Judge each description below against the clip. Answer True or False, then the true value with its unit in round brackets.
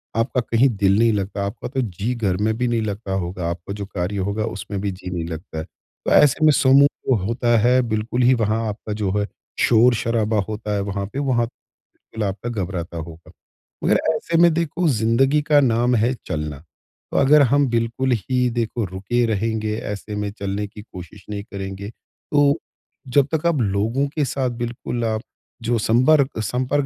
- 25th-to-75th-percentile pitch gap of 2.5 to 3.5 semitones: False (3.9 semitones)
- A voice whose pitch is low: True (110 Hz)